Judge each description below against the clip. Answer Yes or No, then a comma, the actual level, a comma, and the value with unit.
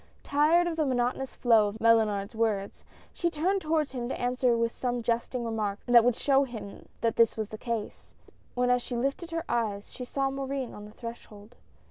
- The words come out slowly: No, average, 195 wpm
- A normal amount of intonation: Yes, average, 3.4 semitones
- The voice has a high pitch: Yes, high, 240 Hz